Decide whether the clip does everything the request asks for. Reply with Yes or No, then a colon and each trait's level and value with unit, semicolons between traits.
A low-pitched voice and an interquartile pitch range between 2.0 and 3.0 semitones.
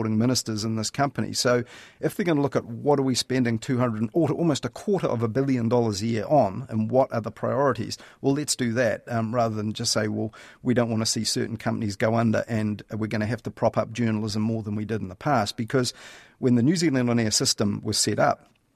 Yes: low, 115 Hz; narrow, 2.5 semitones